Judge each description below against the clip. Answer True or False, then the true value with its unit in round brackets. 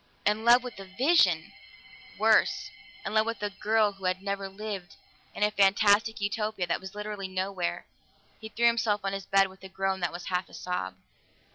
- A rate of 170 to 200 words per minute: True (190 wpm)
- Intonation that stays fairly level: True (2.1 semitones)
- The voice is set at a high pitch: True (200 Hz)